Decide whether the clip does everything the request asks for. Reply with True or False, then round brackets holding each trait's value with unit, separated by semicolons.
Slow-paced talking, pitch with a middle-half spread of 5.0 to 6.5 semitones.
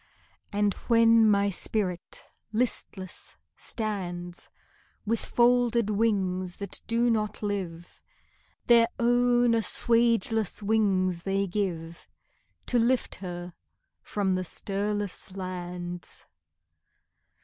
False (90 wpm; 3.8 semitones)